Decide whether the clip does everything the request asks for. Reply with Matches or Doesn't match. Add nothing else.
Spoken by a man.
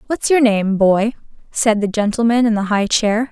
Doesn't match